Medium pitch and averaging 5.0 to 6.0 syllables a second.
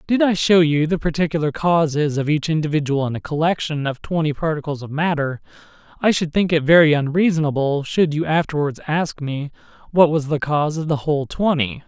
Yes: medium, 155 Hz; 5.6 syllables/s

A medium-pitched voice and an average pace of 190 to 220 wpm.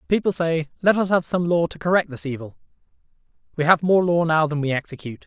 Yes: medium, 165 Hz; fast, 205 wpm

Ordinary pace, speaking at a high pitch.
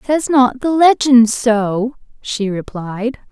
No: slow, 125 wpm; high, 240 Hz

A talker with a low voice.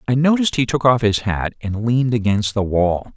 Yes: low, 115 Hz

